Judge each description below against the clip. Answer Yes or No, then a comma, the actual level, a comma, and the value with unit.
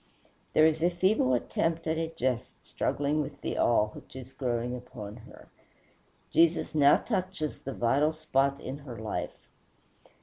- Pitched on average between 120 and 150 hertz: Yes, medium, 140 Hz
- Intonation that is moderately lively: Yes, average, 4.4 semitones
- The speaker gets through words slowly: No, average, 155 wpm